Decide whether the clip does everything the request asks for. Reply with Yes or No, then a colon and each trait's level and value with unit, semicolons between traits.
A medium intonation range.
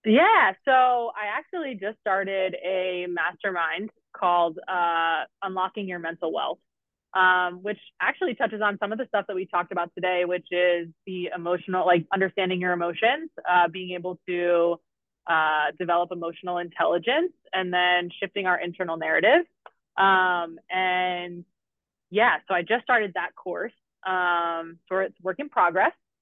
No: narrow, 2.0 semitones